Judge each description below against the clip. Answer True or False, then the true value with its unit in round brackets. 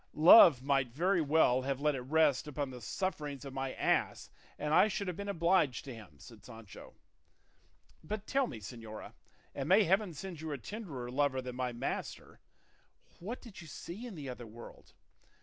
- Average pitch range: False (6.1 semitones)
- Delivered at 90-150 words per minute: False (185 wpm)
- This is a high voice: False (145 Hz)